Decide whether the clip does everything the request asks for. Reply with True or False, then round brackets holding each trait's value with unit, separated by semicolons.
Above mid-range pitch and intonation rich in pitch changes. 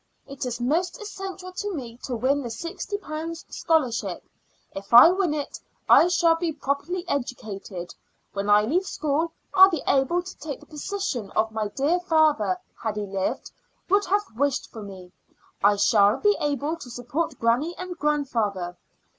True (285 Hz; 7.3 semitones)